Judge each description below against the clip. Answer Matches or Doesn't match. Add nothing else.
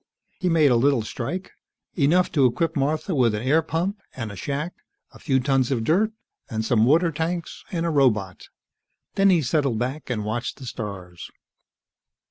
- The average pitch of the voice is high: Doesn't match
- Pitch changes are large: Matches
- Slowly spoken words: Doesn't match